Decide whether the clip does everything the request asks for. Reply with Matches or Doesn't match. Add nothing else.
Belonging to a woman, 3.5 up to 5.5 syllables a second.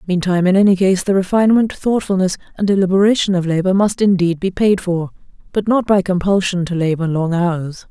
Doesn't match